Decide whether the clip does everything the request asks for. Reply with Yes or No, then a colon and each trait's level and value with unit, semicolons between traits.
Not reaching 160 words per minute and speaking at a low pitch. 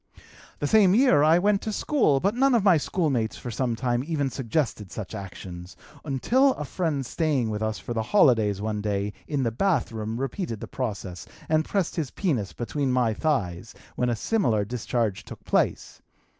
No: average, 180 wpm; low, 130 Hz